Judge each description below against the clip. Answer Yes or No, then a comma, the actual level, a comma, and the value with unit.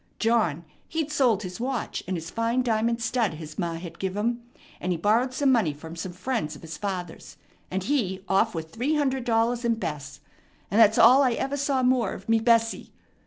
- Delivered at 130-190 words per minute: No, fast, 205 wpm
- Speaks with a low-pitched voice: No, high, 225 Hz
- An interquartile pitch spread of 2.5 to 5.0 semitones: No, wide, 5.5 semitones